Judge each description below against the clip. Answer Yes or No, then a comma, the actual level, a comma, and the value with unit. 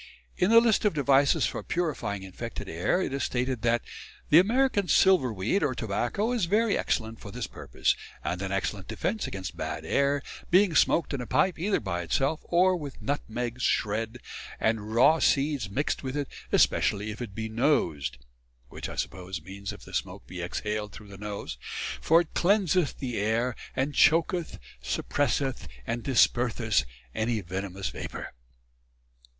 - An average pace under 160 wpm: No, average, 165 wpm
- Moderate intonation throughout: No, wide, 7.5 semitones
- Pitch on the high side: No, low, 125 Hz